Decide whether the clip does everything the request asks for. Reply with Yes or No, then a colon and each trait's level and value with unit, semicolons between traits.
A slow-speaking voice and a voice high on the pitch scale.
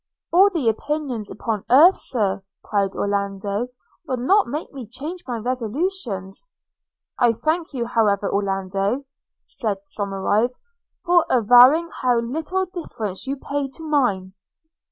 Yes: slow, 125 wpm; high, 245 Hz